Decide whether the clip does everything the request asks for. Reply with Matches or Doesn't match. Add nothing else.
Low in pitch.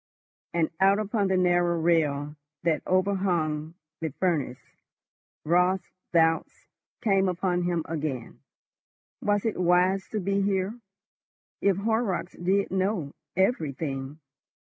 Doesn't match